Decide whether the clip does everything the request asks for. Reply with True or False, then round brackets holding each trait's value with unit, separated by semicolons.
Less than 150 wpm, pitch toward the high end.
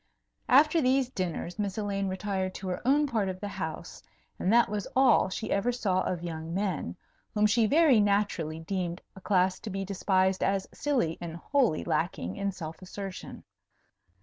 False (175 wpm; 195 Hz)